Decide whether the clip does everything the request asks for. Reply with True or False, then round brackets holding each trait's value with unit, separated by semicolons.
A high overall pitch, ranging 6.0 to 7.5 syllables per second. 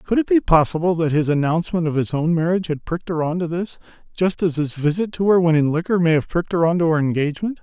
False (170 Hz; 6.6 syllables/s)